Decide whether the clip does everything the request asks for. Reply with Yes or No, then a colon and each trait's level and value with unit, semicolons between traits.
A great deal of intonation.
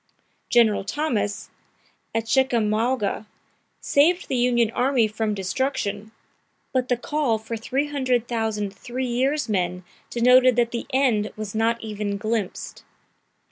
No: average, 3.2 semitones